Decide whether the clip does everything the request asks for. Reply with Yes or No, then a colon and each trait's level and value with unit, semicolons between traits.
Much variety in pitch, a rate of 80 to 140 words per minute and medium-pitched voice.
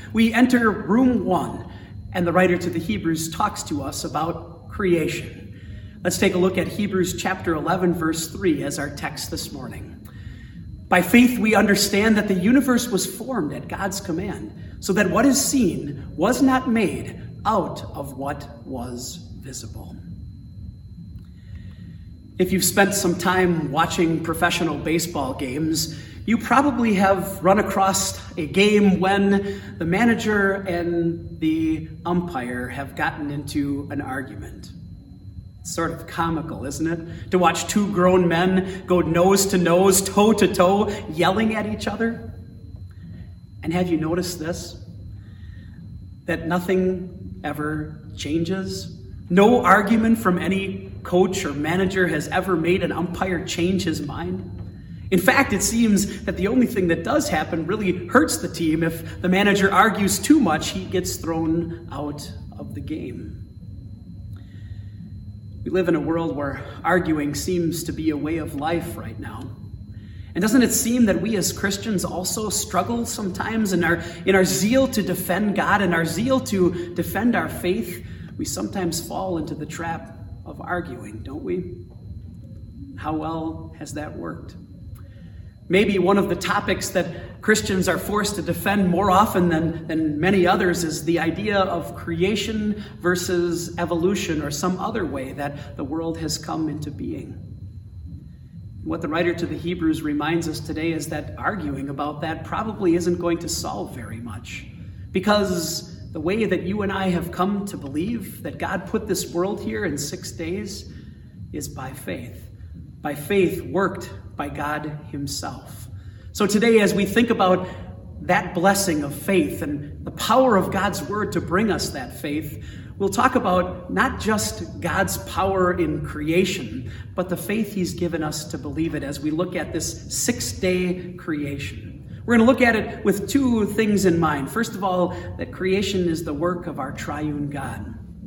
No: wide, 6.5 semitones; average, 160 wpm; medium, 170 Hz